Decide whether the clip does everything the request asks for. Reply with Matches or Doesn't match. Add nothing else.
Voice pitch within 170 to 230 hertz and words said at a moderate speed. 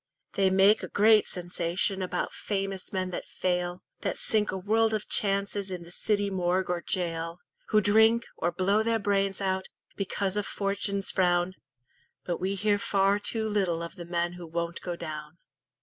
Matches